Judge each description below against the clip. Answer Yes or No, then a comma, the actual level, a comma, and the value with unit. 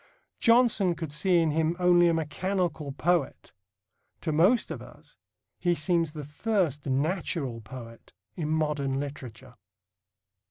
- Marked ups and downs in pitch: No, average, 3.7 semitones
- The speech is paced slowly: Yes, slow, 125 wpm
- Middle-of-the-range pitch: Yes, medium, 160 Hz